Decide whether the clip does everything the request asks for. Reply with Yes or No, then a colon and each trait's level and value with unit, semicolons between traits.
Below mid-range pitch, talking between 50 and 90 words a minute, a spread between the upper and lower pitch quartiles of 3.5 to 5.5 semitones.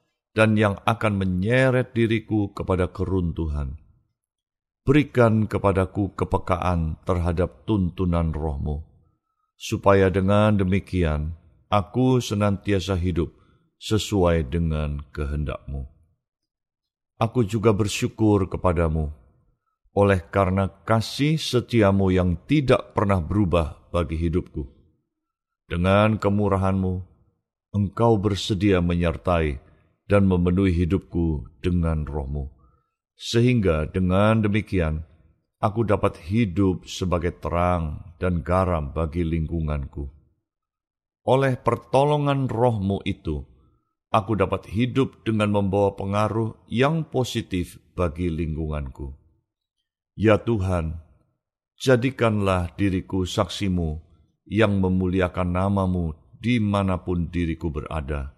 Yes: very low, 95 Hz; slow, 85 wpm; average, 4.6 semitones